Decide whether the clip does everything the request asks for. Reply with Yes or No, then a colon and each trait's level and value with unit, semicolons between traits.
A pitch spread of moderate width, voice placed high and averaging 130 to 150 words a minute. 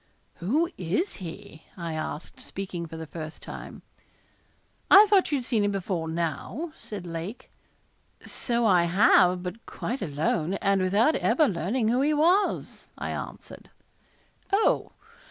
No: wide, 7.1 semitones; high, 195 Hz; average, 140 wpm